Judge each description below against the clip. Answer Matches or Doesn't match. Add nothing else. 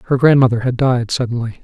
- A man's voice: Matches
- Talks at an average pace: Matches